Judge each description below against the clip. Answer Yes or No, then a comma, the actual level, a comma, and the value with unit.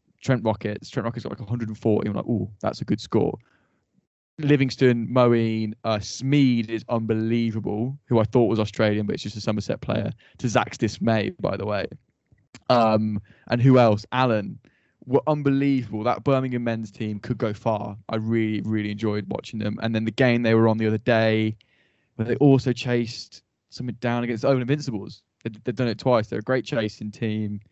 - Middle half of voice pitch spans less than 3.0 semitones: Yes, narrow, 2.5 semitones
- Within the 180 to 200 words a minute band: Yes, average, 185 wpm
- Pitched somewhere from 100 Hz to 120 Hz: Yes, low, 115 Hz